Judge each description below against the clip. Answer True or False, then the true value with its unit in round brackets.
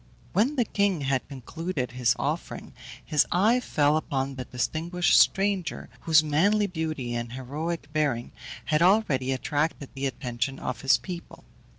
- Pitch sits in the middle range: True (150 Hz)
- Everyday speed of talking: True (145 wpm)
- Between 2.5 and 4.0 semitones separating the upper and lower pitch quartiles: False (4.9 semitones)